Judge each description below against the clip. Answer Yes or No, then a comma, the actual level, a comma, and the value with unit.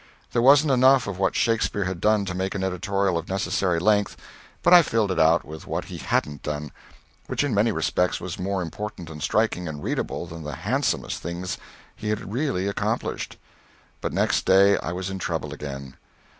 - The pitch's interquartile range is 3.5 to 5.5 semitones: Yes, average, 3.9 semitones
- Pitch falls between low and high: No, very low, 95 Hz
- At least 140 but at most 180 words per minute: No, average, 195 wpm